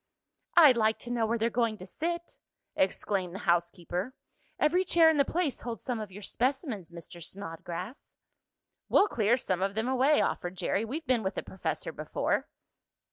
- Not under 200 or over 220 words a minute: No, average, 175 wpm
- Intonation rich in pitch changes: Yes, wide, 5.9 semitones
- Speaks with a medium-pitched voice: No, high, 225 Hz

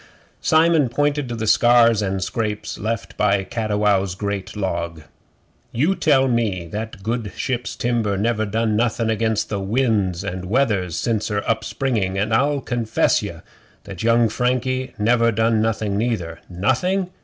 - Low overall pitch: Yes, low, 110 Hz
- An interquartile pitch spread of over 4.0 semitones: No, average, 3.2 semitones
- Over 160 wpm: No, average, 150 wpm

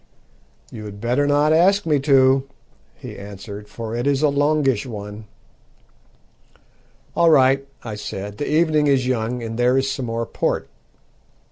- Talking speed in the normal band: Yes, average, 150 wpm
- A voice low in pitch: Yes, low, 130 Hz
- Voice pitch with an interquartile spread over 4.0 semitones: Yes, average, 4.5 semitones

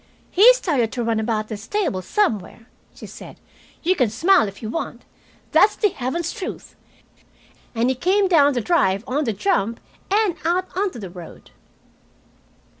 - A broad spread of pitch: Yes, wide, 9.0 semitones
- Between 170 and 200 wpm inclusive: No, average, 160 wpm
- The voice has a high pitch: Yes, very high, 260 Hz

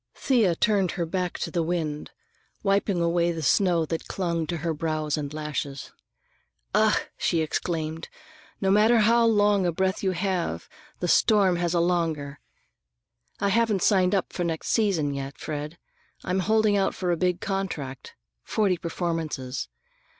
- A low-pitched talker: No, medium, 175 Hz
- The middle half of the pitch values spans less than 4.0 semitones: Yes, average, 3.6 semitones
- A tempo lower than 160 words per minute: Yes, average, 150 wpm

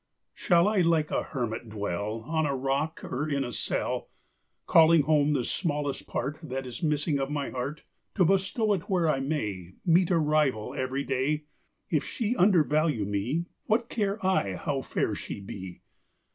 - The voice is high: No, medium, 150 Hz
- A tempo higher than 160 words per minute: Yes, average, 170 wpm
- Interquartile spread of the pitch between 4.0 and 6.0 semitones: Yes, average, 4.6 semitones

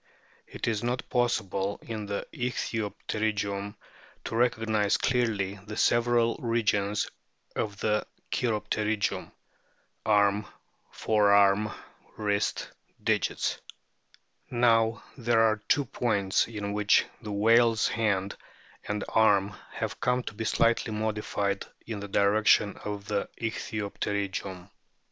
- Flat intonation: Yes, narrow, 2.0 semitones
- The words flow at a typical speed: No, slow, 105 wpm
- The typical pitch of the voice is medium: No, low, 105 Hz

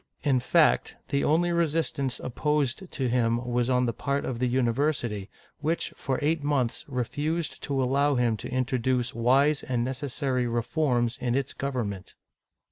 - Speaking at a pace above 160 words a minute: No, average, 150 wpm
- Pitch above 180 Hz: No, low, 130 Hz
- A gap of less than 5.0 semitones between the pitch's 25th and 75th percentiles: Yes, average, 3.1 semitones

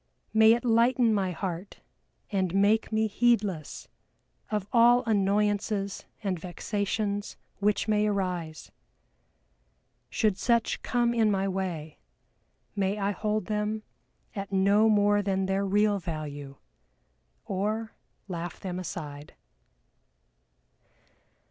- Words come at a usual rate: No, slow, 105 wpm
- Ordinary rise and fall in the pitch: No, narrow, 2.3 semitones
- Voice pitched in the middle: No, high, 200 Hz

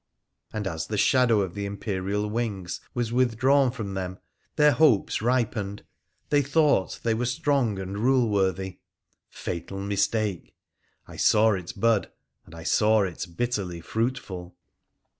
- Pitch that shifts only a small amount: No, average, 4.2 semitones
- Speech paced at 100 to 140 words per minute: Yes, slow, 135 wpm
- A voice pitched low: Yes, low, 105 Hz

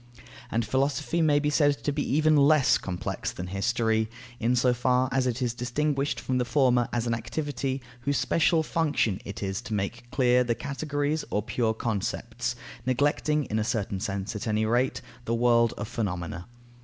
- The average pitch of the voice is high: No, low, 125 Hz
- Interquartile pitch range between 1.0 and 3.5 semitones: No, average, 4.3 semitones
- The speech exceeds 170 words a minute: Yes, average, 180 wpm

